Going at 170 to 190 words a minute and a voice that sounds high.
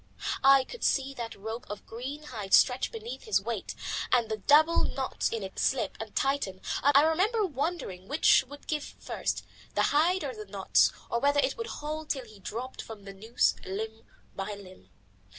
Yes: average, 185 wpm; very high, 255 Hz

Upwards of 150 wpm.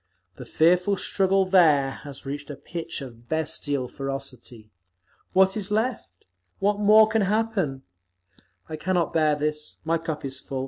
No: average, 145 wpm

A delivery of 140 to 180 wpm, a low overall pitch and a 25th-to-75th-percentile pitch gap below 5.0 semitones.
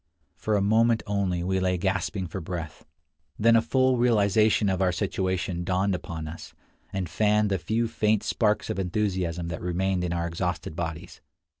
Yes: average, 170 wpm; very low, 95 Hz; average, 3.4 semitones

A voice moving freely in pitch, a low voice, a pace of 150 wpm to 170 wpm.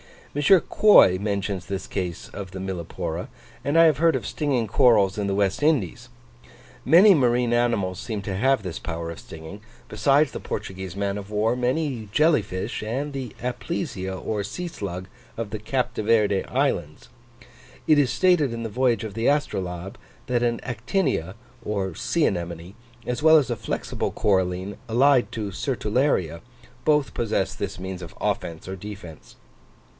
Yes: wide, 5.7 semitones; low, 110 Hz; average, 165 wpm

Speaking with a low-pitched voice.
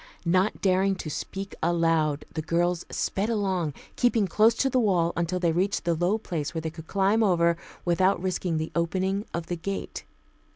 No: medium, 180 Hz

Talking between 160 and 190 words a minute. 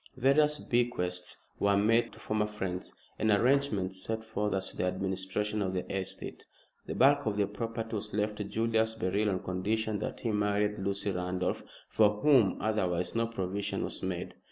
Yes: average, 175 wpm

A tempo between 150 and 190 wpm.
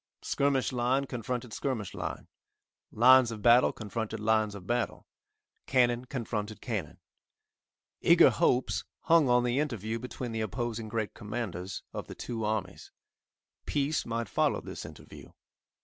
No: slow, 135 wpm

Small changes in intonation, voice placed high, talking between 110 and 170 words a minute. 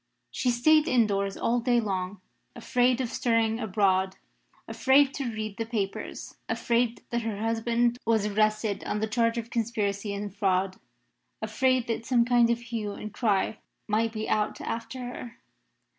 Yes: narrow, 2.3 semitones; high, 225 Hz; average, 155 wpm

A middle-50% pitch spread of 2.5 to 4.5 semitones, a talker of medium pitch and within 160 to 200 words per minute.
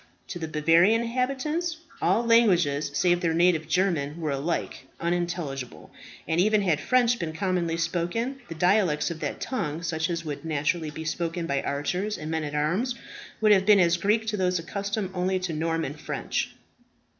Yes: average, 4.1 semitones; medium, 175 Hz; average, 170 wpm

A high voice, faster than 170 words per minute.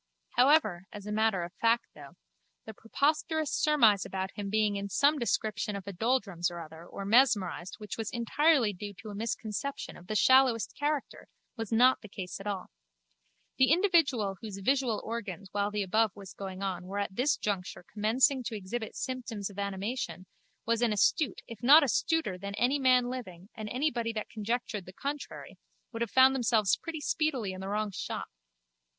Yes: high, 220 Hz; average, 180 wpm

